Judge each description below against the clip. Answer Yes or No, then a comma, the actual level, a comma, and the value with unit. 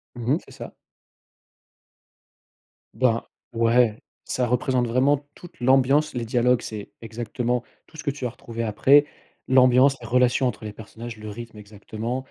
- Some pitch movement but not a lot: No, narrow, 2.3 semitones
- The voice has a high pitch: No, low, 120 Hz